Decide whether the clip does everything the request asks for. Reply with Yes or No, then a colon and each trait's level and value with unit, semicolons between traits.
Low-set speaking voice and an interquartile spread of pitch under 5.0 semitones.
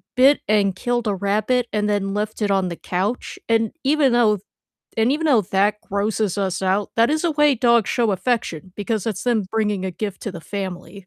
No: high, 210 Hz; average, 3.3 semitones